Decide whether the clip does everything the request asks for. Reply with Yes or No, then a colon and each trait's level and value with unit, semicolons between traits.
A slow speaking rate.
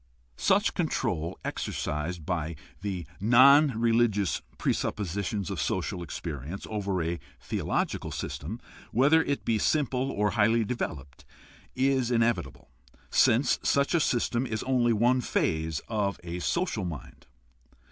Yes: slow, 120 wpm